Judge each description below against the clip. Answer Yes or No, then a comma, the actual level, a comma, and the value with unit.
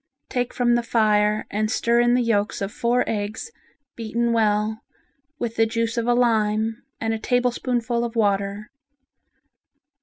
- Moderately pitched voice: No, high, 225 Hz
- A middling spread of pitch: No, narrow, 2.0 semitones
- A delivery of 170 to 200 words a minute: No, average, 150 wpm